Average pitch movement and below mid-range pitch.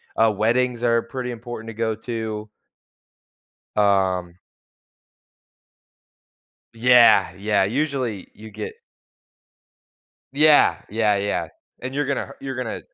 Yes: average, 3.1 semitones; low, 115 Hz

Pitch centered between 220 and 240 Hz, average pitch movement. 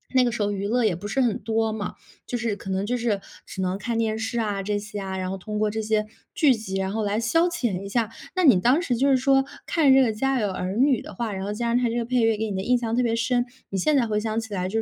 Yes: high, 225 Hz; average, 3.2 semitones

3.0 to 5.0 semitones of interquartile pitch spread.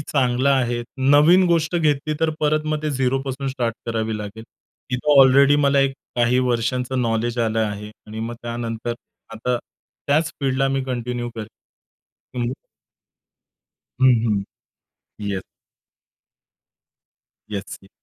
Yes: average, 3.3 semitones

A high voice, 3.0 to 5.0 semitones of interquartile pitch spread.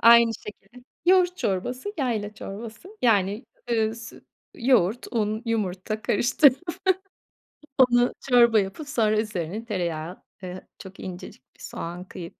Yes: high, 220 Hz; average, 4.0 semitones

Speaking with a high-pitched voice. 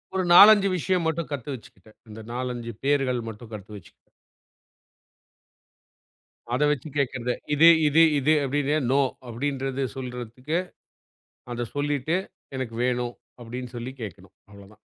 No: low, 125 Hz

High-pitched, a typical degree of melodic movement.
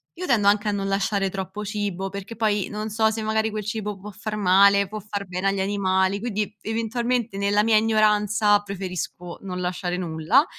No: high, 205 Hz; narrow, 1.9 semitones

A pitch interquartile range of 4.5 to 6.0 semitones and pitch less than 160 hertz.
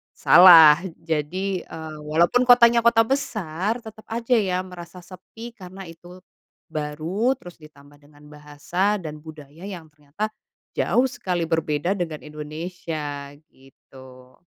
No: average, 4.8 semitones; medium, 170 Hz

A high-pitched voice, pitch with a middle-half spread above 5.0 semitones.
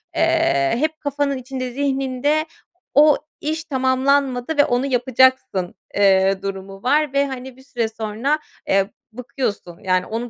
No: very high, 260 Hz; average, 4.5 semitones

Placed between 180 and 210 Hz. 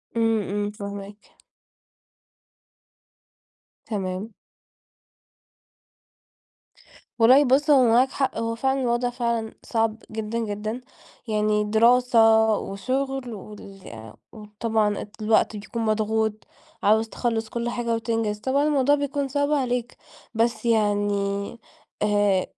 No: high, 225 Hz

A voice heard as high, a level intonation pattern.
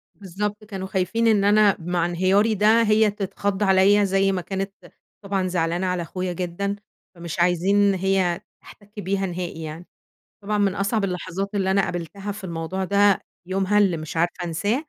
Yes: high, 195 Hz; narrow, 2.3 semitones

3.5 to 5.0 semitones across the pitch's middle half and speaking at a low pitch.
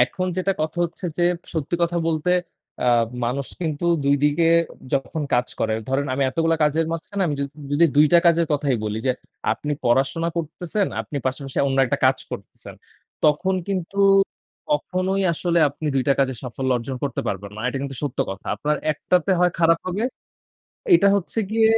No: average, 4.2 semitones; medium, 155 Hz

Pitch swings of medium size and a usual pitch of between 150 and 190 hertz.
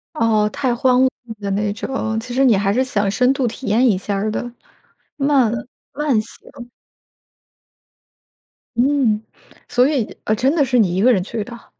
No: average, 3.7 semitones; high, 240 Hz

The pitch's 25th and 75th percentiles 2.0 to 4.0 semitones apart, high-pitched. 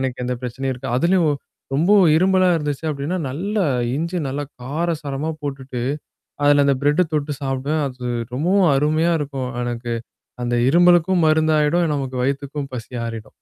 No: average, 3.6 semitones; medium, 145 Hz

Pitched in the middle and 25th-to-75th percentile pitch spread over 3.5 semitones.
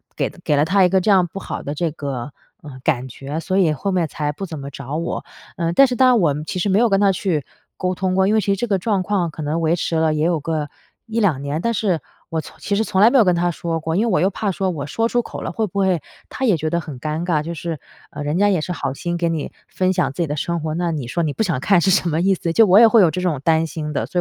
Yes: medium, 170 Hz; average, 4.0 semitones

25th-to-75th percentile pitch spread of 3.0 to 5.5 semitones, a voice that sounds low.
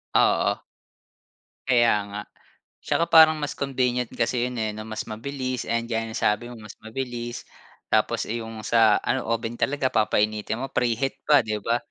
No: narrow, 2.6 semitones; low, 120 Hz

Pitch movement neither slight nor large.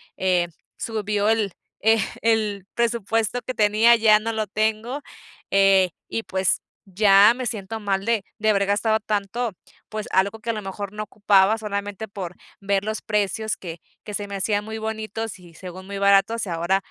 No: narrow, 2.1 semitones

